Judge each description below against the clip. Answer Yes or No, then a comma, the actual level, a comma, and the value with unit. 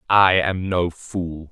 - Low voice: Yes, very low, 90 Hz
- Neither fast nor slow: Yes, average, 160 wpm